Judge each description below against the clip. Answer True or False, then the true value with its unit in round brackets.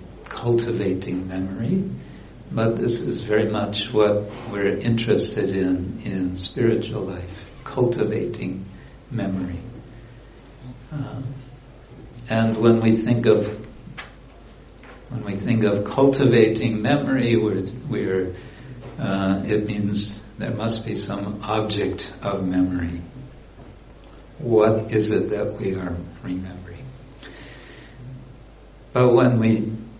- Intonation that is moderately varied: True (3.5 semitones)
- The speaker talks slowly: True (100 wpm)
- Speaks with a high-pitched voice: False (110 Hz)